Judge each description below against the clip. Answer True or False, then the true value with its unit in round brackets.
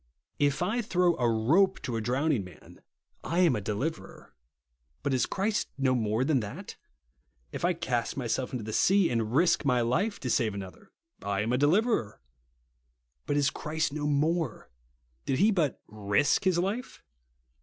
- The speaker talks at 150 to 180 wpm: True (170 wpm)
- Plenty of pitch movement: True (7.1 semitones)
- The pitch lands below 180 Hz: True (140 Hz)